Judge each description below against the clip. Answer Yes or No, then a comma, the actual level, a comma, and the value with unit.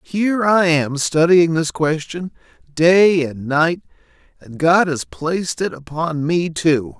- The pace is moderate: Yes, average, 145 wpm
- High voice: No, medium, 165 Hz